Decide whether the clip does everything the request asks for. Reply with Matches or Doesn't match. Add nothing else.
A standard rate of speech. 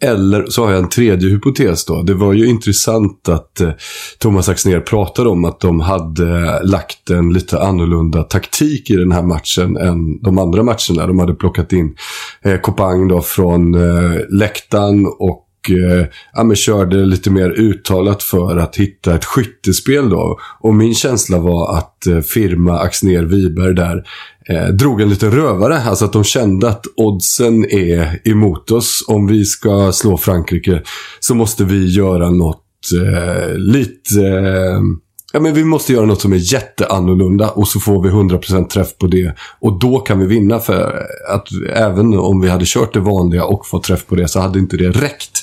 Matches